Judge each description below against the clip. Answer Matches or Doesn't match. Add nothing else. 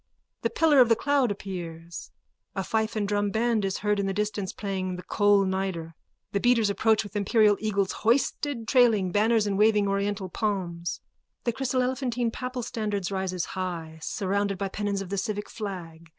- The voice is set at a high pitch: Matches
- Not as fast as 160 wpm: Doesn't match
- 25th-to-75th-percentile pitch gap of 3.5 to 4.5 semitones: Doesn't match